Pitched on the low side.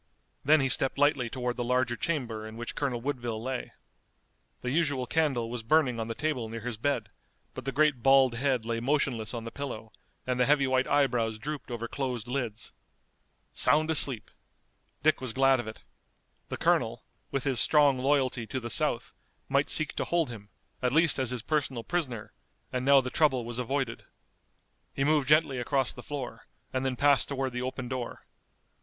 Yes: low, 130 Hz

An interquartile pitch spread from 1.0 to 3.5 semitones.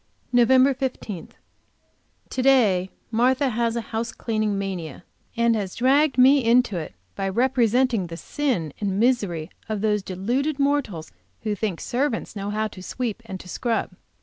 No: average, 4.7 semitones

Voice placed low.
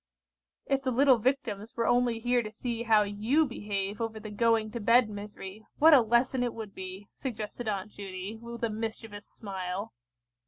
No: high, 225 Hz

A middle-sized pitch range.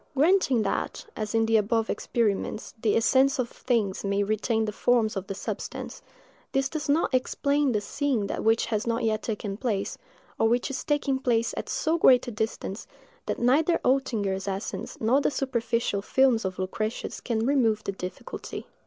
Yes: average, 3.8 semitones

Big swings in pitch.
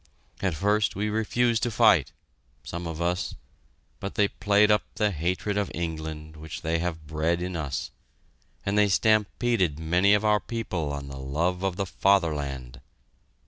No: average, 4.8 semitones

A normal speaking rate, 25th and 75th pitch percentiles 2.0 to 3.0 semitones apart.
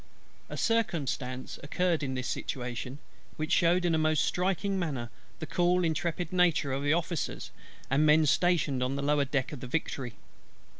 No: average, 160 wpm; average, 4.5 semitones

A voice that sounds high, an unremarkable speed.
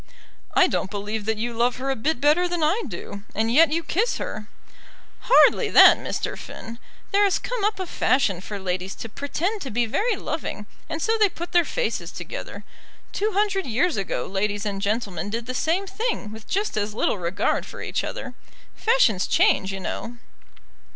Yes: very high, 255 Hz; average, 190 wpm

